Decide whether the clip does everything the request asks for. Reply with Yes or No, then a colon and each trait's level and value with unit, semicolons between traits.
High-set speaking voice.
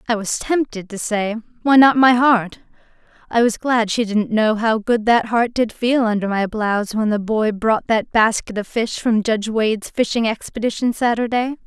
Yes: high, 225 Hz